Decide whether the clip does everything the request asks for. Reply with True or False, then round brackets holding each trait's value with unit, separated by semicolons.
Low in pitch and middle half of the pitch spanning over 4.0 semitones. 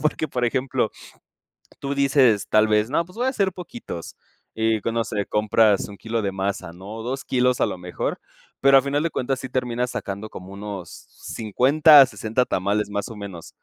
True (115 Hz; 4.8 semitones)